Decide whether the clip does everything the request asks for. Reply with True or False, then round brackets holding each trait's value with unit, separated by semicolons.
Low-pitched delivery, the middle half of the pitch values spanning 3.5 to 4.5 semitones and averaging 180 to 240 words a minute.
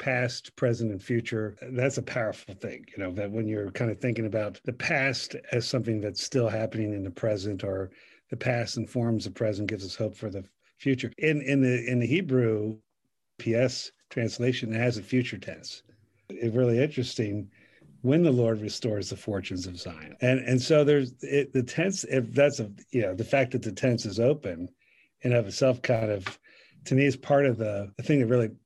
False (120 Hz; 3.1 semitones; 205 wpm)